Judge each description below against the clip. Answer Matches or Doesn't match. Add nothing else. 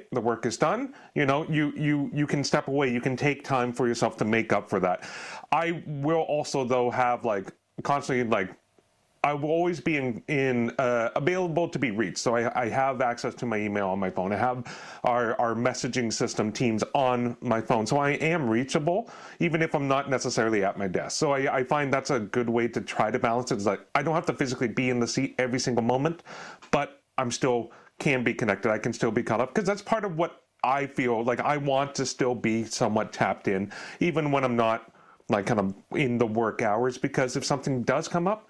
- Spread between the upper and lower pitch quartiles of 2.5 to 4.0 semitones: Matches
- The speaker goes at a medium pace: Doesn't match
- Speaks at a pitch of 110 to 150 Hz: Matches